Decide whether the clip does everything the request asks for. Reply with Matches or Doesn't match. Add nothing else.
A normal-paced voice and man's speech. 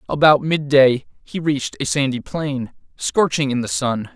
Matches